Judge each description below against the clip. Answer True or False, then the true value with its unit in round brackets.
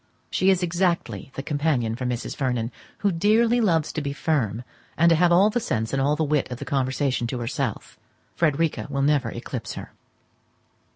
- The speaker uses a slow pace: False (185 wpm)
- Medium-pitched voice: True (145 Hz)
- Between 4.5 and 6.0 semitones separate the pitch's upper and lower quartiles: True (5.2 semitones)